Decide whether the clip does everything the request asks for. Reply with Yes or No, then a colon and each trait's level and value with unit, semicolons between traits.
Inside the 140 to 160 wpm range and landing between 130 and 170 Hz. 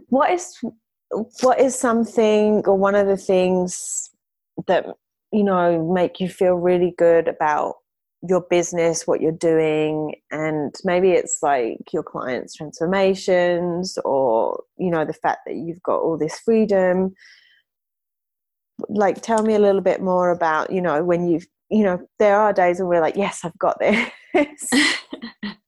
No: average, 155 wpm; medium, 185 Hz